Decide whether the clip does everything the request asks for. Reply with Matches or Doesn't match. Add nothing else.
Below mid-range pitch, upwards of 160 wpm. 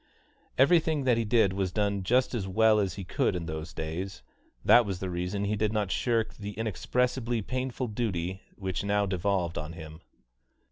Matches